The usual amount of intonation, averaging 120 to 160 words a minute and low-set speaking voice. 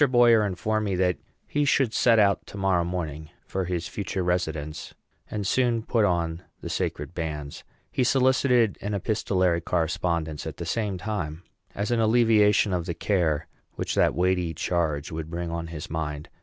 No: average, 4.6 semitones; average, 170 wpm; very low, 90 Hz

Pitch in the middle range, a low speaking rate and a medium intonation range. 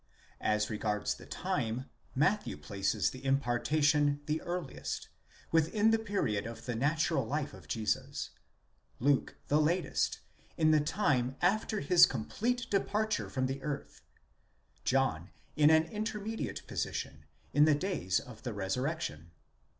No: medium, 145 Hz; slow, 125 wpm; wide, 6.6 semitones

